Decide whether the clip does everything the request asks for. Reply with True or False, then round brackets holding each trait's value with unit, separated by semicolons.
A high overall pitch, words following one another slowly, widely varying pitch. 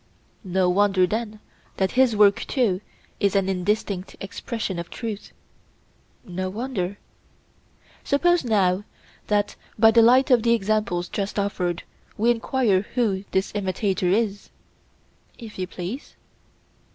False (205 Hz; 125 wpm; 3.4 semitones)